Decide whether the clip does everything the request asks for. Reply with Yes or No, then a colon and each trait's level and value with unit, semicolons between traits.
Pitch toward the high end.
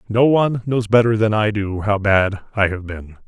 No: low, 105 Hz